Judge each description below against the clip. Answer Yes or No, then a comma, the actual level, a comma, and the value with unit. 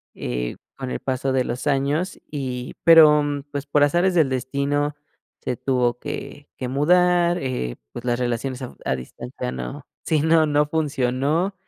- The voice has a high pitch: No, medium, 140 Hz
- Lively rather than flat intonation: No, average, 3.4 semitones